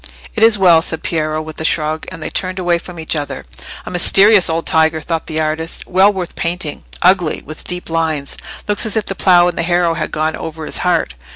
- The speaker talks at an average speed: No, fast, 210 wpm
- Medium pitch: Yes, medium, 165 Hz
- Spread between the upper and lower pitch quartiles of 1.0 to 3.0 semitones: Yes, narrow, 2.4 semitones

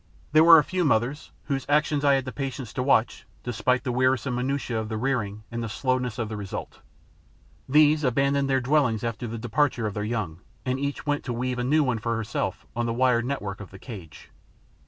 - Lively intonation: No, average, 3.4 semitones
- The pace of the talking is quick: Yes, fast, 220 wpm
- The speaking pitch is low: Yes, low, 125 Hz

